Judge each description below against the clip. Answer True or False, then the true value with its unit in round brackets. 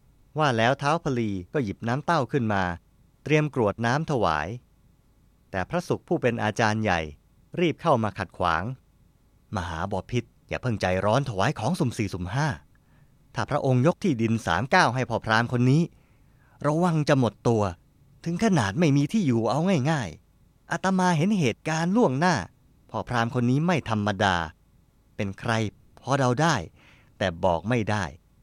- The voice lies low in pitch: True (125 Hz)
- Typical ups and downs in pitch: False (5.8 semitones)